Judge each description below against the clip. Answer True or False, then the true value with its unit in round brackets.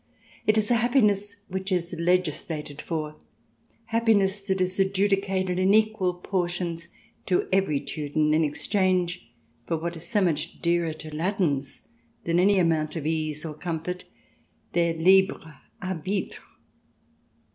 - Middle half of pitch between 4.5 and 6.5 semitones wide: False (3.2 semitones)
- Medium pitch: True (180 Hz)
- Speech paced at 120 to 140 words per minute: True (135 wpm)